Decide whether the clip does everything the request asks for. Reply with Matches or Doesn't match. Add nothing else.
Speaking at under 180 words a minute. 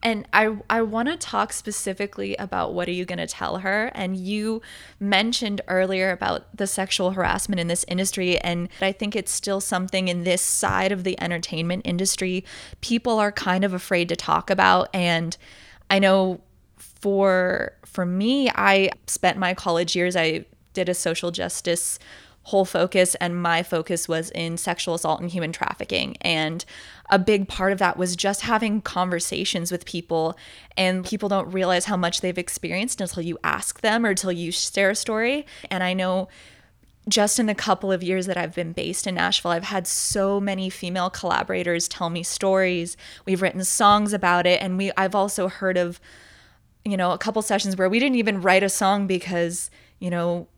Doesn't match